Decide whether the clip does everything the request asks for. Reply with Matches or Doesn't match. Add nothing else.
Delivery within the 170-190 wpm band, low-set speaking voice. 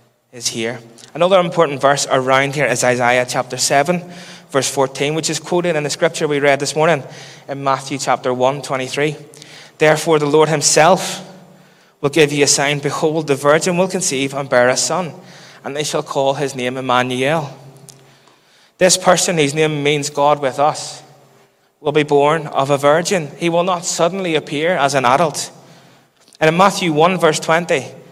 Doesn't match